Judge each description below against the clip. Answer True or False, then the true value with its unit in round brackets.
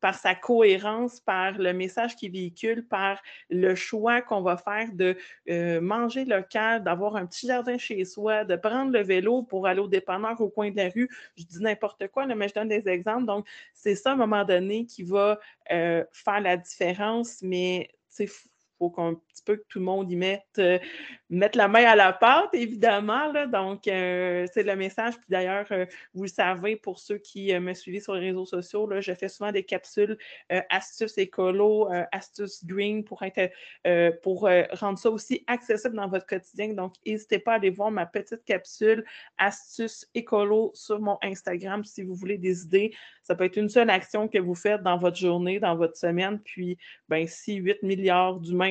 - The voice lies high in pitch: True (200 Hz)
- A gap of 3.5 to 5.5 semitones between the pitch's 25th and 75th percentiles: False (2.7 semitones)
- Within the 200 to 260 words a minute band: True (205 wpm)